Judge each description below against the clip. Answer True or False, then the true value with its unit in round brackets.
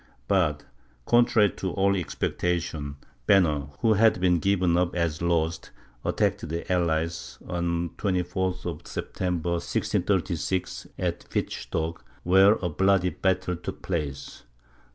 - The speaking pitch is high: False (90 Hz)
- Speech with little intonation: True (2.1 semitones)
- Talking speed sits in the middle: False (120 wpm)